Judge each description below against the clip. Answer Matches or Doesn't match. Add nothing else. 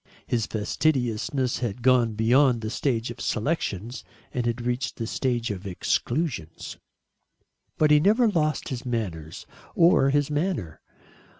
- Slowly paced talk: Matches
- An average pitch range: Matches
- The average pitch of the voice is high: Doesn't match